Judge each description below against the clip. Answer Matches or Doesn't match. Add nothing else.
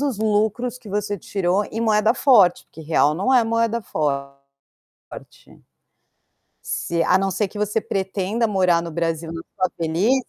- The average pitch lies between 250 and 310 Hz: Doesn't match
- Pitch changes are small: Doesn't match